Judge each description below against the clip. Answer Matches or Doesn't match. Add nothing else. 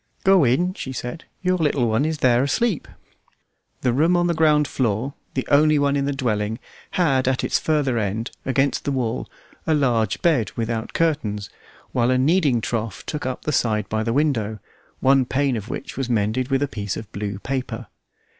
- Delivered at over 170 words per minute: Matches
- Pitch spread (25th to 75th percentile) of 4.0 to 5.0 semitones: Matches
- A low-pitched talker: Matches